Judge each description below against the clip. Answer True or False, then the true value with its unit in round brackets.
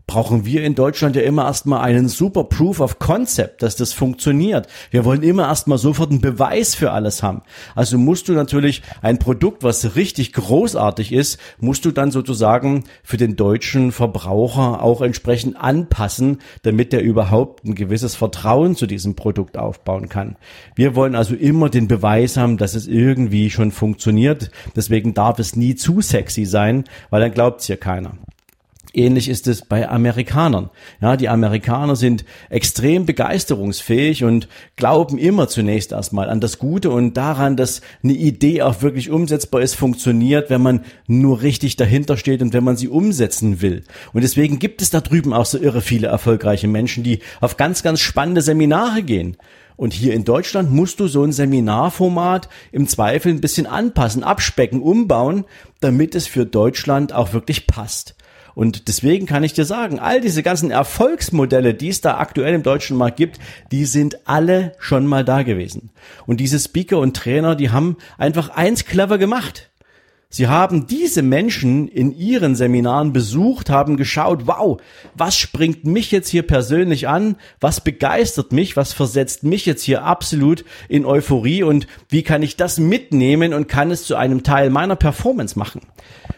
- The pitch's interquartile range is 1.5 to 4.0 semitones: False (4.9 semitones)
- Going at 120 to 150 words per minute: False (170 wpm)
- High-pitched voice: False (130 Hz)